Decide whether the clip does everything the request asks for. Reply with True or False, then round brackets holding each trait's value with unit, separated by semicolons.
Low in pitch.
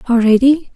False (255 Hz)